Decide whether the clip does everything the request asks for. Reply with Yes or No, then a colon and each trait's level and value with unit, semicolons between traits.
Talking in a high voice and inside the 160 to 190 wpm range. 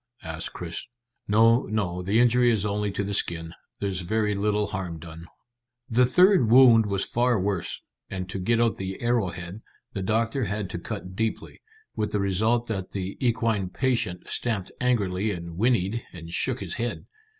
No: low, 105 Hz; average, 170 wpm